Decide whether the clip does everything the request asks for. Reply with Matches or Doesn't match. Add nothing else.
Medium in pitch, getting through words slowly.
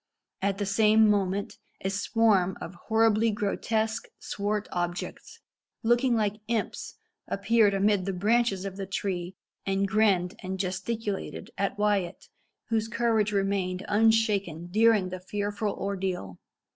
Doesn't match